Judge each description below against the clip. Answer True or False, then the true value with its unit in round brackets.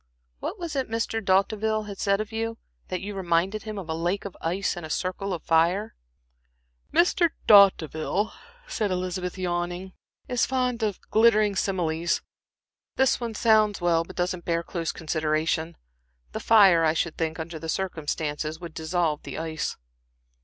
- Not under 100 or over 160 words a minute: True (155 wpm)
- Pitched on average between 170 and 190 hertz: True (185 Hz)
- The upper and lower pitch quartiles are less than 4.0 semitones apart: False (4.4 semitones)